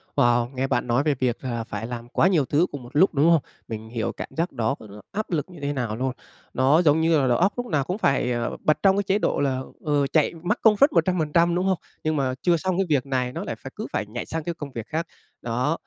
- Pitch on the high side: No, medium, 145 Hz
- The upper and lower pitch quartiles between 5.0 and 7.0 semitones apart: Yes, wide, 5.6 semitones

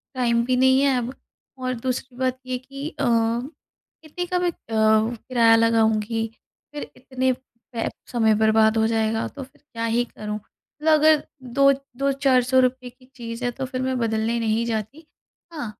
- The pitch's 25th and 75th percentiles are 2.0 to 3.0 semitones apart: Yes, narrow, 2.5 semitones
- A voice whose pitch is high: Yes, high, 245 Hz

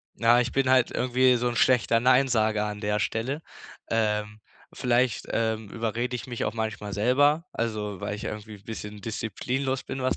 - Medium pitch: No, low, 115 Hz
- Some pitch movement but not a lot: Yes, average, 3.0 semitones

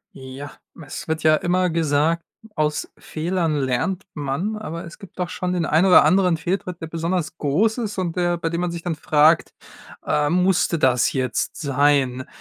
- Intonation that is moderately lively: Yes, average, 3.4 semitones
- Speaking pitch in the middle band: Yes, medium, 165 Hz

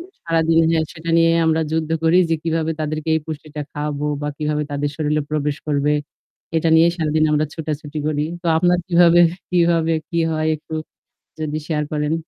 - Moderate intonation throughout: No, narrow, 1.5 semitones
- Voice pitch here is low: No, medium, 155 Hz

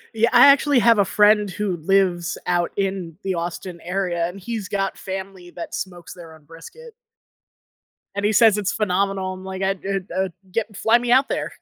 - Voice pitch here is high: Yes, high, 195 Hz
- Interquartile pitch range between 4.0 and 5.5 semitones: No, average, 2.7 semitones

